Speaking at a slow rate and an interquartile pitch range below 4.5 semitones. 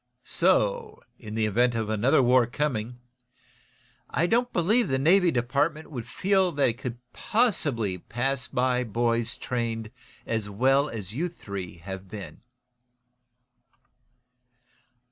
No: slow, 125 wpm; average, 5.3 semitones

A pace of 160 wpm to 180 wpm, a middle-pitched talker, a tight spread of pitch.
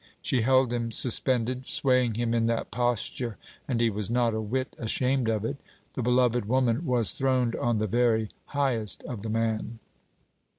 No: average, 170 wpm; low, 120 Hz; narrow, 2.1 semitones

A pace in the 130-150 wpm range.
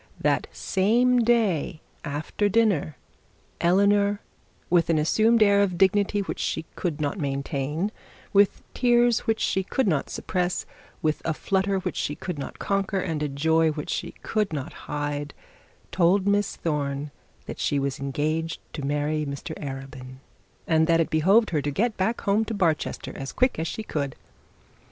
No: average, 160 wpm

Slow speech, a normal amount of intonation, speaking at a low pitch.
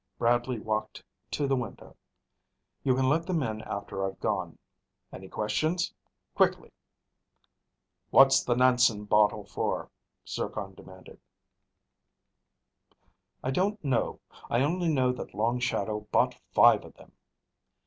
Yes: slow, 120 wpm; average, 4.3 semitones; low, 125 Hz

